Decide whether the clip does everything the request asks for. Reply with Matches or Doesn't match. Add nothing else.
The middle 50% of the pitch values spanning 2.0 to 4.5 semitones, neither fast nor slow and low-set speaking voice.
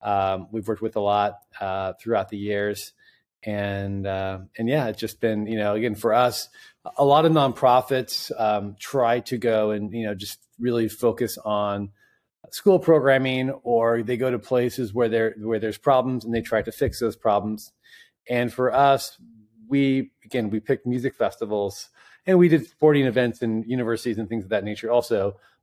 Matches